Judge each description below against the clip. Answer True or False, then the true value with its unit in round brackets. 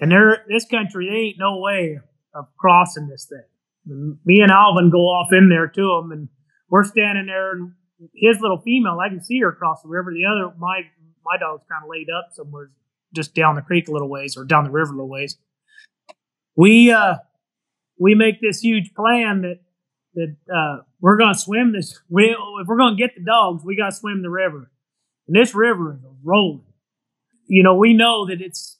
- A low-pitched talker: False (180 Hz)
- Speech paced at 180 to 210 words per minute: True (205 wpm)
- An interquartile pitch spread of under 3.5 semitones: False (4.5 semitones)